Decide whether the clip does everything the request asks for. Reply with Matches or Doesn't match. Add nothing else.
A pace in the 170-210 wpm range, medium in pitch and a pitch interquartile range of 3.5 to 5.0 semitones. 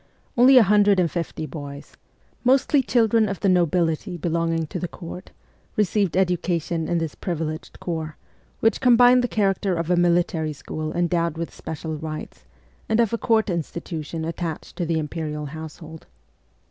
Doesn't match